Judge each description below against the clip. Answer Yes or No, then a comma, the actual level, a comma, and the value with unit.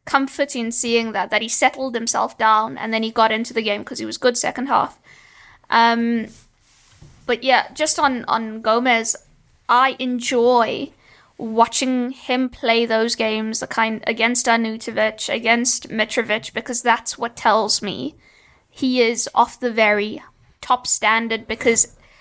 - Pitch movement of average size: No, narrow, 1.9 semitones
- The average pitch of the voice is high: Yes, high, 230 Hz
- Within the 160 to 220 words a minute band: No, average, 150 wpm